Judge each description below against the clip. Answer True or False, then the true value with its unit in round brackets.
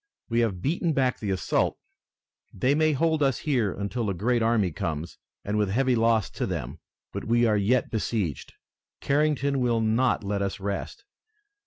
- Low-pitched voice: True (115 Hz)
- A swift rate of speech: False (170 wpm)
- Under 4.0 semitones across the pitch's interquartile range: False (4.7 semitones)